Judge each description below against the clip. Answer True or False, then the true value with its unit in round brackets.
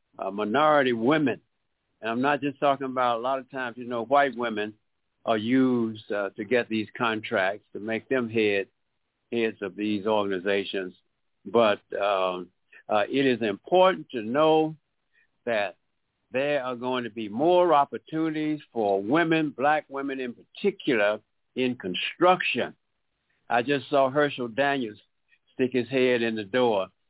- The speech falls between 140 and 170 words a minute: True (150 wpm)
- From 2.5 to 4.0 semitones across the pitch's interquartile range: False (4.5 semitones)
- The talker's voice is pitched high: False (125 Hz)